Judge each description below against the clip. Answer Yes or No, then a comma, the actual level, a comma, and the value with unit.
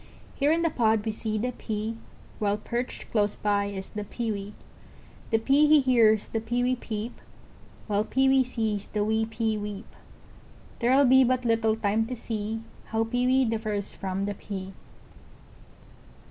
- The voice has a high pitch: Yes, high, 225 Hz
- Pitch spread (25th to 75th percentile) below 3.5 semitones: Yes, average, 2.9 semitones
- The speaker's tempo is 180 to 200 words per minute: No, average, 155 wpm